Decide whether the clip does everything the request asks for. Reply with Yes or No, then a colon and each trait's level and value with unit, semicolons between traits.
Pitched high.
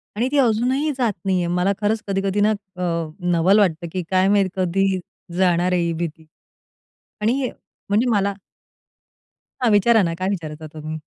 Yes: high, 195 Hz